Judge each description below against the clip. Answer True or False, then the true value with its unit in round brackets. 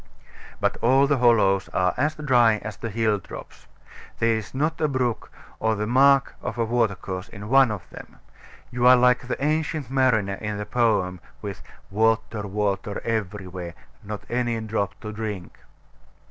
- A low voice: True (110 Hz)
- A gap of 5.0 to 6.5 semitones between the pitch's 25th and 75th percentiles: False (3.5 semitones)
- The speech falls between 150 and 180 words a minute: True (165 wpm)